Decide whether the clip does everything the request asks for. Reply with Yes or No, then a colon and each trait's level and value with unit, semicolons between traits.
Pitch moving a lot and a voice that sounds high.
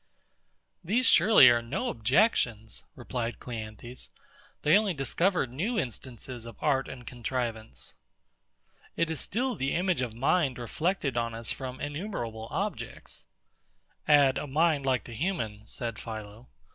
No: wide, 5.8 semitones; low, 130 Hz